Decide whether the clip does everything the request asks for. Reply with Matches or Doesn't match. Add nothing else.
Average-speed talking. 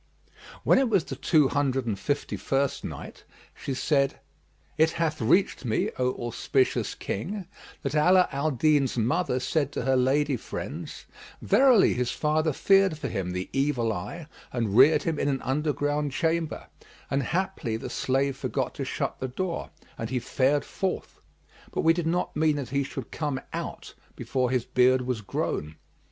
Matches